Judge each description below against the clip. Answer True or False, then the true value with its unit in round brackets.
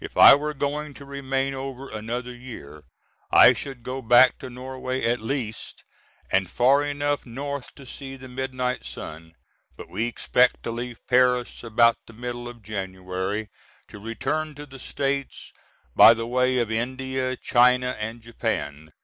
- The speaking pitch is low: True (125 Hz)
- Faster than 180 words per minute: False (160 wpm)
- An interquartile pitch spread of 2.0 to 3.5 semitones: True (2.6 semitones)